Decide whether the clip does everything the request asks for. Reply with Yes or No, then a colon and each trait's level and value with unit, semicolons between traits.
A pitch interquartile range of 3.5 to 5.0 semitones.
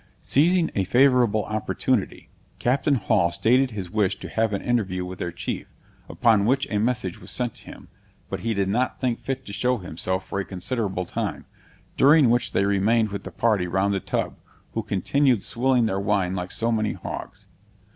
Yes: average, 4.4 semitones